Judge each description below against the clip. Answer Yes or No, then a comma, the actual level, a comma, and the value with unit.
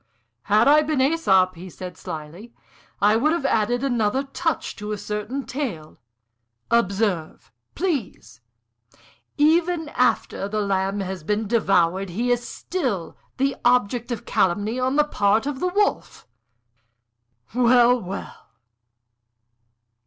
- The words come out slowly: Yes, slow, 125 wpm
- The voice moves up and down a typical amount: No, wide, 5.7 semitones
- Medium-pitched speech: No, high, 230 Hz